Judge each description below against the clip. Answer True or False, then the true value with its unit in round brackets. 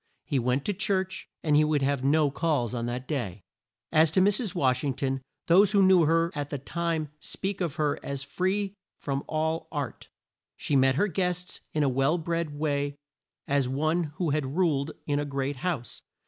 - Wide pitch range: False (3.8 semitones)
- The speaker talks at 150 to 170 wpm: False (190 wpm)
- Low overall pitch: False (150 Hz)